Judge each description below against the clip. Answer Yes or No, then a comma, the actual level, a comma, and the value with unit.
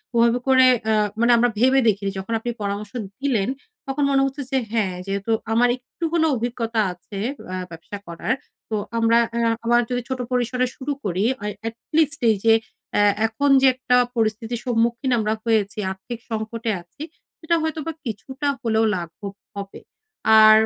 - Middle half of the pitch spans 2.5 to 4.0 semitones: Yes, average, 3.1 semitones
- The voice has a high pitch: Yes, high, 230 Hz